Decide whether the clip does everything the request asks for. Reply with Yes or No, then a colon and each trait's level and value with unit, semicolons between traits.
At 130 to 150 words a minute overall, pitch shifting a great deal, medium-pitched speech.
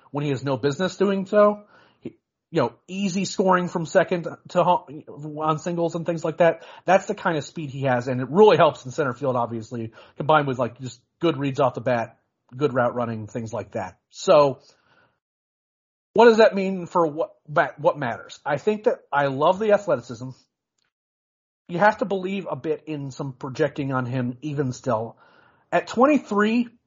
No: average, 190 wpm; wide, 6.4 semitones; medium, 155 Hz